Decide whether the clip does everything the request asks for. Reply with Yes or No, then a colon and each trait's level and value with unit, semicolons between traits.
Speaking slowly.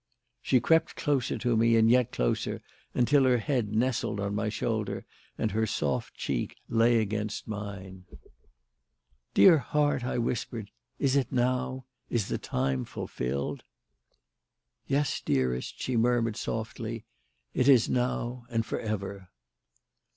Yes: slow, 130 wpm